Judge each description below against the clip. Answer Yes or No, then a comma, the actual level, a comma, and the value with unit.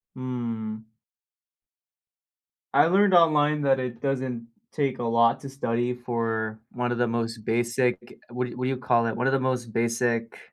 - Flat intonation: Yes, narrow, 2.3 semitones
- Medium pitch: No, low, 120 Hz